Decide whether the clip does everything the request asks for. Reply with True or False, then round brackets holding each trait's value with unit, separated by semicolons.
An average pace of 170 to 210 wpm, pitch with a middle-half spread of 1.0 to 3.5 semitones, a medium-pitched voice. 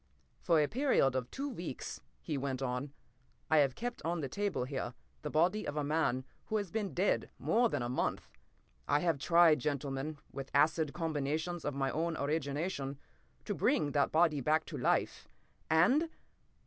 False (175 wpm; 3.9 semitones; 155 Hz)